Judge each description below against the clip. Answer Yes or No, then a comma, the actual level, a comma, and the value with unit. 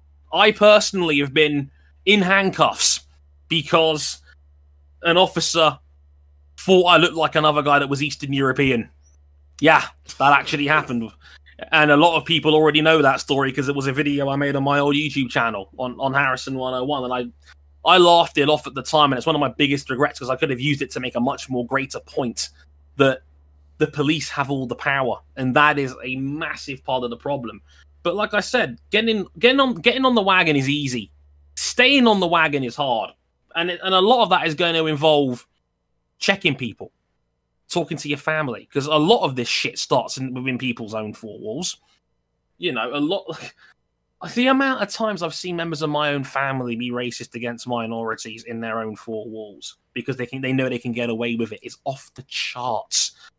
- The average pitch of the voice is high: No, medium, 140 Hz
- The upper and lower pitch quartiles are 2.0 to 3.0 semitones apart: No, average, 5.3 semitones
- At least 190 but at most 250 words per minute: Yes, fast, 205 wpm